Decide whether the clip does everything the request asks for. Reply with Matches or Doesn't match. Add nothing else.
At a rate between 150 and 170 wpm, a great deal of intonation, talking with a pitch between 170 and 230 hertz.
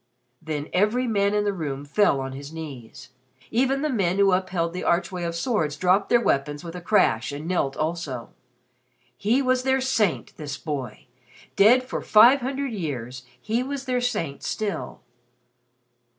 Matches